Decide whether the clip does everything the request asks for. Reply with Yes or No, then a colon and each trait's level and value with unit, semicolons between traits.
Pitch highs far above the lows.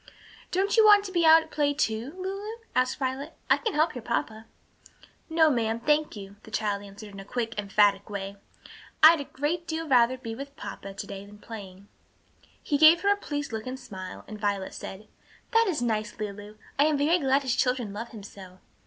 Yes: wide, 7.0 semitones